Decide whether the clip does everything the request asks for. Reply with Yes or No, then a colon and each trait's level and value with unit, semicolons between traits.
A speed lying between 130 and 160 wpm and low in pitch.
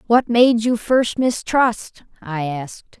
No: average, 140 wpm; high, 225 Hz